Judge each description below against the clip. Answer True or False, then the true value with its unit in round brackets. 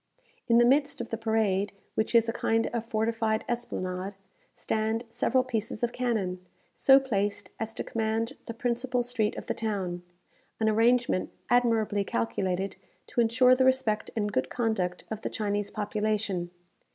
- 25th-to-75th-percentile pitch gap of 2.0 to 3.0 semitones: True (2.5 semitones)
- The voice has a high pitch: True (220 Hz)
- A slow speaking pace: False (155 wpm)